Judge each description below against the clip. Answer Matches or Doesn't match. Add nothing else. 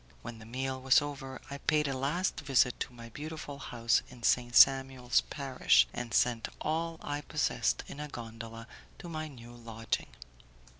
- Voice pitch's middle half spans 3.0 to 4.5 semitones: Matches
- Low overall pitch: Matches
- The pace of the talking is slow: Doesn't match